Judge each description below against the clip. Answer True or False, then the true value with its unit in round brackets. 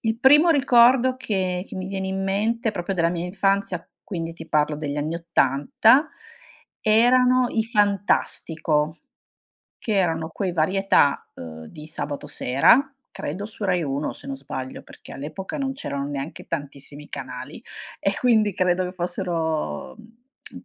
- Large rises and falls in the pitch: True (6.3 semitones)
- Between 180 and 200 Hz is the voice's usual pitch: True (185 Hz)